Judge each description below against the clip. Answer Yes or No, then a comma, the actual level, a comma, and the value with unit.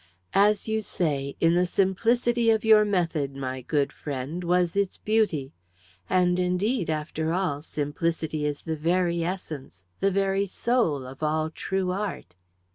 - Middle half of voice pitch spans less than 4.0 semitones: No, average, 4.6 semitones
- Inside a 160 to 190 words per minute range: No, average, 150 wpm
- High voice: No, medium, 175 Hz